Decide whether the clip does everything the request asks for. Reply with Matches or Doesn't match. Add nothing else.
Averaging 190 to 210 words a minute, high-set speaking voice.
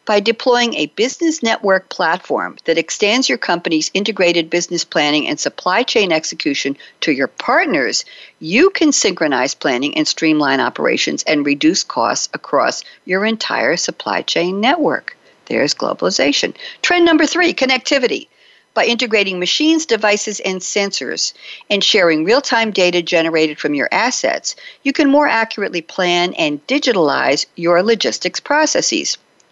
Doesn't match